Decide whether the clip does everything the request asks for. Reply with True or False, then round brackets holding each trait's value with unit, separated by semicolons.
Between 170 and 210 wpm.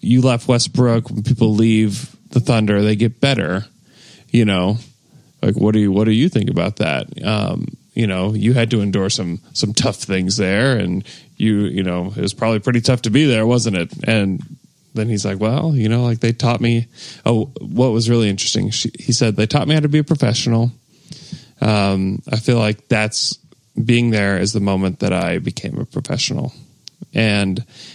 True (200 wpm)